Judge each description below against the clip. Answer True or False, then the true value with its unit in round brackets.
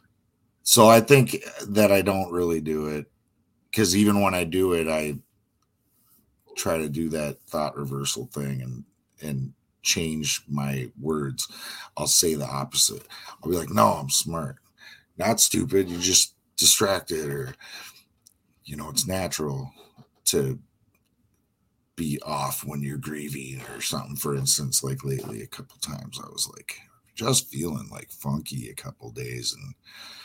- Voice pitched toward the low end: True (75 Hz)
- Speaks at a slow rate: False (145 wpm)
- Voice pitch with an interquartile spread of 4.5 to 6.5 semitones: True (5.5 semitones)